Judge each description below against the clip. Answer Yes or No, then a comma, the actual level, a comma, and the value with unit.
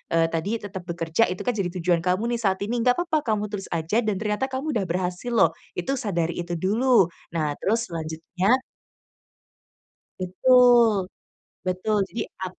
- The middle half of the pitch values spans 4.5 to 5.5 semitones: Yes, average, 5.0 semitones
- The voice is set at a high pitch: Yes, high, 195 Hz